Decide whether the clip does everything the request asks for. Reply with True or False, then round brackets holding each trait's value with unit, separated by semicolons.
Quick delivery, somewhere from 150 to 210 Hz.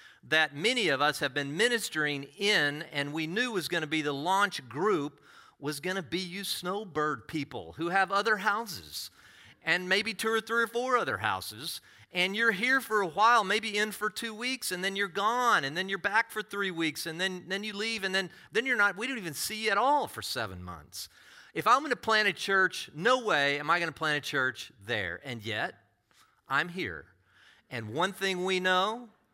True (210 wpm; 190 Hz)